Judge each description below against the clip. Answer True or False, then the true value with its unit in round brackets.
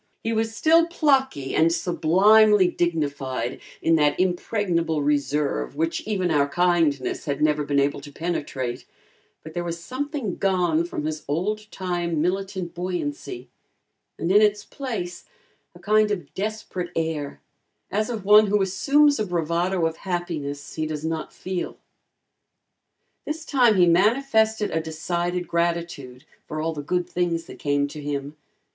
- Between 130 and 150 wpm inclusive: True (145 wpm)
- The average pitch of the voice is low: False (175 Hz)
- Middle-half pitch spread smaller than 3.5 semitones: False (5.0 semitones)